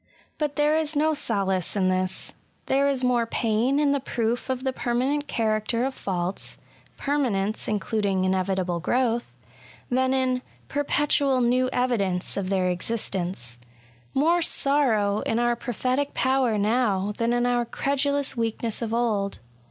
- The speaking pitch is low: No, high, 240 Hz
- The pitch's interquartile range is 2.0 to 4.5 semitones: No, average, 4.9 semitones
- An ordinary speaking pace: Yes, average, 145 wpm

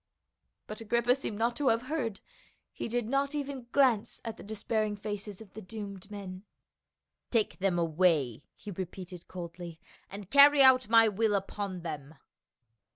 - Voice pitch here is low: No, high, 210 Hz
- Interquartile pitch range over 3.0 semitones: Yes, average, 4.3 semitones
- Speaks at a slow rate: No, average, 155 wpm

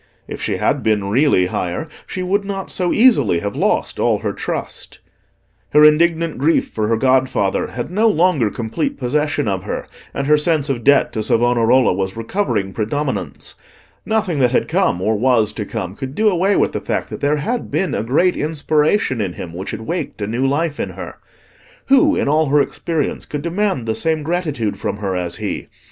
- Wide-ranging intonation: Yes, wide, 7.0 semitones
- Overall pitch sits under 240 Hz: Yes, medium, 140 Hz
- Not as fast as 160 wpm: No, average, 195 wpm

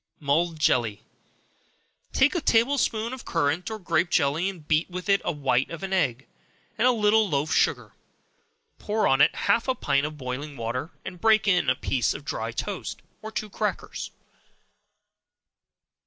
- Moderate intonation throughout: No, wide, 7.2 semitones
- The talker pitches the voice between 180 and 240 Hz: No, medium, 170 Hz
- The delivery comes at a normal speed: Yes, average, 170 wpm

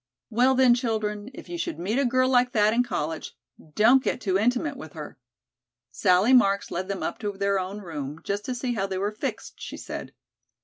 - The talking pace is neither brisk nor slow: No, fast, 210 wpm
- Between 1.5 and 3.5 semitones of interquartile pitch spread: No, average, 4.3 semitones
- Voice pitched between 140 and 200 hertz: No, high, 210 Hz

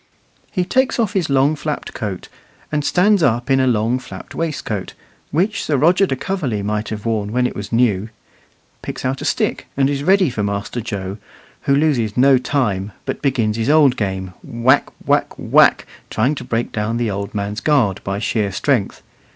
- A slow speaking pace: No, average, 185 wpm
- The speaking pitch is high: No, low, 125 Hz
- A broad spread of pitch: Yes, wide, 5.7 semitones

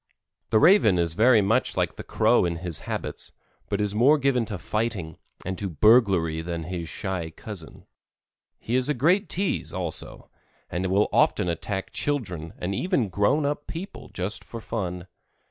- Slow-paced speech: No, average, 165 wpm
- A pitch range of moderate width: No, wide, 6.0 semitones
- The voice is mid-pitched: No, low, 100 Hz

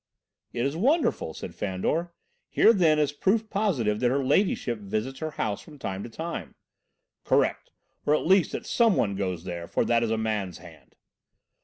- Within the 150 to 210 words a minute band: Yes, average, 180 wpm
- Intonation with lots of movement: Yes, wide, 8.6 semitones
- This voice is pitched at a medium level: No, low, 130 Hz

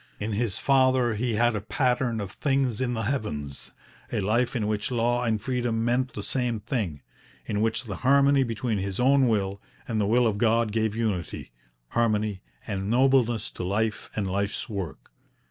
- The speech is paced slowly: No, average, 180 wpm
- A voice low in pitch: Yes, low, 115 Hz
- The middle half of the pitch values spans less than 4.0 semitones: Yes, average, 3.1 semitones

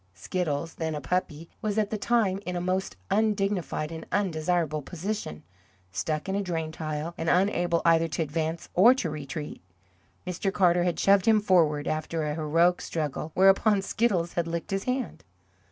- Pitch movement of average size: Yes, average, 3.7 semitones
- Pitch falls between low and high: Yes, medium, 170 Hz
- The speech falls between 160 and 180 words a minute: Yes, average, 170 wpm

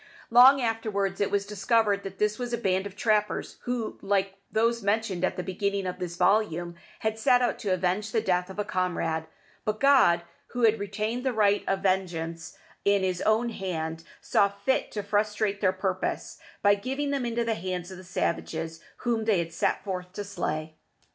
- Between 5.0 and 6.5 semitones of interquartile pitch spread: No, average, 3.2 semitones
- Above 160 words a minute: Yes, average, 190 wpm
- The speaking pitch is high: Yes, high, 200 Hz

